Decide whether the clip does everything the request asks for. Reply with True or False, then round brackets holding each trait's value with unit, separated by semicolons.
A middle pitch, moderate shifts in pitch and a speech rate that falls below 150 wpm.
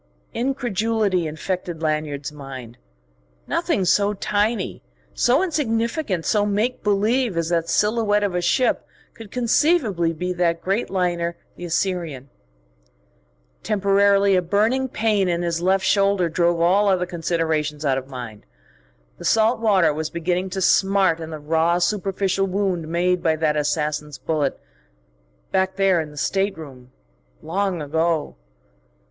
True (180 Hz; 4.0 semitones; 135 wpm)